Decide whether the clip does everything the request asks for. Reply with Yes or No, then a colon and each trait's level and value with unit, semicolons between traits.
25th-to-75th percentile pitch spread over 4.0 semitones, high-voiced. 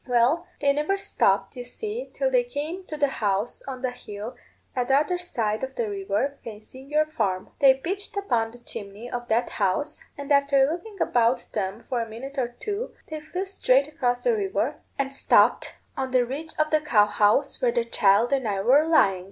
Yes: average, 5.2 semitones; very high, 265 Hz